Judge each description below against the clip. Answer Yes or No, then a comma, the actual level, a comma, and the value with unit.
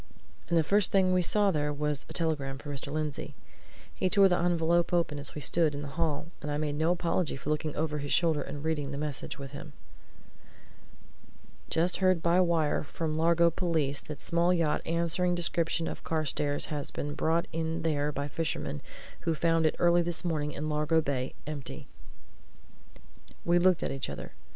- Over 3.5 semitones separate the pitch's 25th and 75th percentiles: No, narrow, 2.6 semitones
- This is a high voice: No, medium, 160 Hz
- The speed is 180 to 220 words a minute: Yes, average, 185 wpm